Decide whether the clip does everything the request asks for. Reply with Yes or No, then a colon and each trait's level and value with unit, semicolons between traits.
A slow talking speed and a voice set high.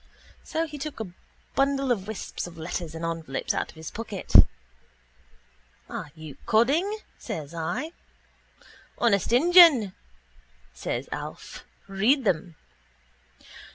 Yes: slow, 115 wpm; high, 215 Hz